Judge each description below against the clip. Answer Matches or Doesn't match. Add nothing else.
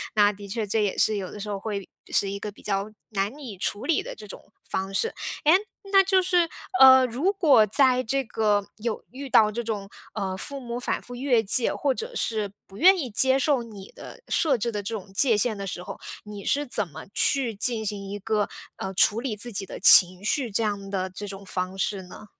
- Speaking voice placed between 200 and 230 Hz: Matches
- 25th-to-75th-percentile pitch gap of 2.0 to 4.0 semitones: Doesn't match